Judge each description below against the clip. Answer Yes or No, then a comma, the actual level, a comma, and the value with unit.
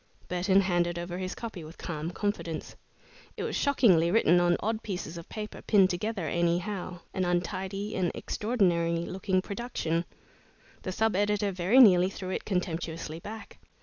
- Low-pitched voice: No, medium, 185 Hz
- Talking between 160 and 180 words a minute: No, average, 150 wpm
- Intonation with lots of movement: No, average, 3.1 semitones